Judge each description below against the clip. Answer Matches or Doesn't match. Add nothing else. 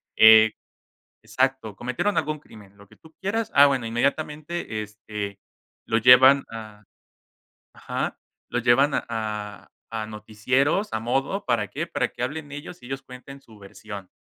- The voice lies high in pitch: Doesn't match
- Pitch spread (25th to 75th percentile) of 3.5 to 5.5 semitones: Matches